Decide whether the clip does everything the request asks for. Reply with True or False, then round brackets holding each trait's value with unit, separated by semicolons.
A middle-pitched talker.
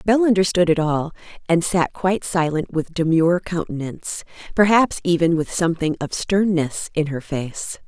True (170 Hz)